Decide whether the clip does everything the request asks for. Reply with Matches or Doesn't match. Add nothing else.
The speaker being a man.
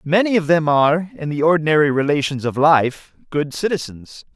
Matches